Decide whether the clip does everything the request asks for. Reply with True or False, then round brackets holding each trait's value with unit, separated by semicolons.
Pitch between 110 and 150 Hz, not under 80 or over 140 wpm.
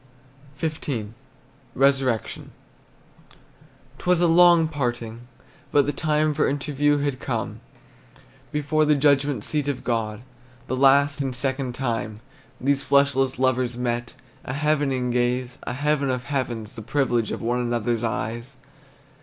True (135 Hz; 135 wpm)